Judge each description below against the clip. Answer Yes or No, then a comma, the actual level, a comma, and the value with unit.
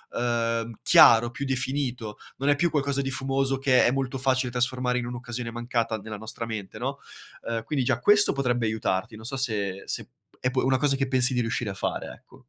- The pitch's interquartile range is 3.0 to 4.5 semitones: No, narrow, 2.5 semitones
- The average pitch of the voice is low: Yes, low, 125 Hz